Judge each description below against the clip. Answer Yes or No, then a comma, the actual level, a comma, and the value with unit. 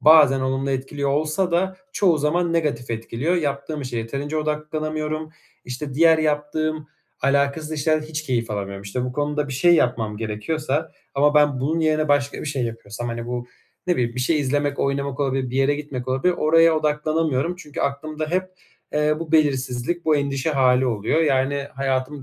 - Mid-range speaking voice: Yes, medium, 145 Hz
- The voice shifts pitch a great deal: No, average, 3.1 semitones